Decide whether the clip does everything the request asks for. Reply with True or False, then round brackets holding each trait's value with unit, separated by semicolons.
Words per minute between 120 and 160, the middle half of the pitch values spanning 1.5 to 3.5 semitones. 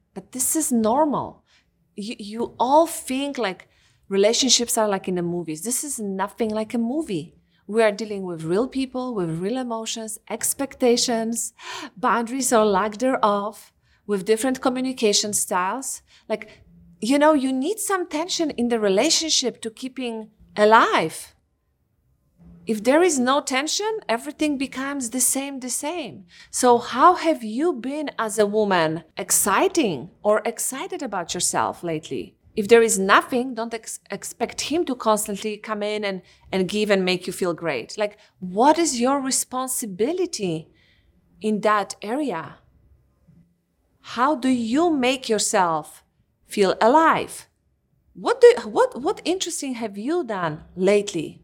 False (145 wpm; 4.9 semitones)